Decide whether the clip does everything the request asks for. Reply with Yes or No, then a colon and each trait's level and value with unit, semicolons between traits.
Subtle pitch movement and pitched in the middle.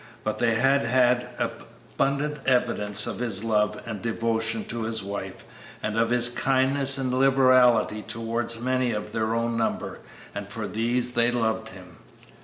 No: narrow, 2.2 semitones; low, 115 Hz